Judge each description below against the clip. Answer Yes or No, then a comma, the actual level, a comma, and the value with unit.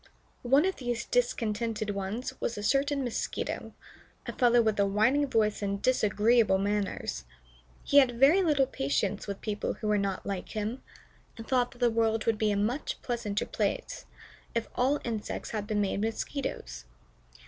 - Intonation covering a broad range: No, average, 3.2 semitones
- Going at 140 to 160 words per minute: No, average, 170 wpm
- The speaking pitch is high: Yes, high, 225 Hz